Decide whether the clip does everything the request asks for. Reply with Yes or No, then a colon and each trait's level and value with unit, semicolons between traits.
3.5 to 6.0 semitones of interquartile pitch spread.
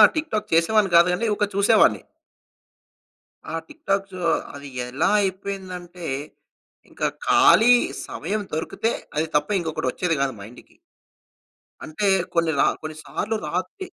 Yes: average, 4.4 semitones